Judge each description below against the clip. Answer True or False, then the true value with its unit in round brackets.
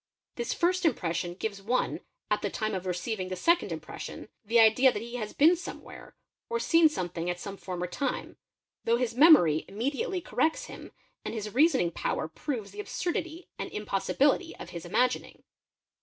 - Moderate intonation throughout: False (8.3 semitones)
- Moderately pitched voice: False (230 Hz)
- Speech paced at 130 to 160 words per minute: False (170 wpm)